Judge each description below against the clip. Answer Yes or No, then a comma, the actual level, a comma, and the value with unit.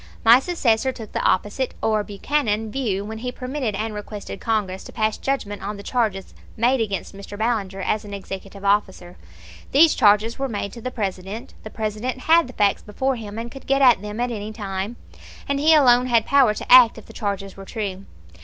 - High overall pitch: Yes, high, 220 Hz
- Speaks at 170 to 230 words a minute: Yes, average, 200 wpm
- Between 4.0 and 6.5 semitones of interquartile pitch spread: No, average, 3.6 semitones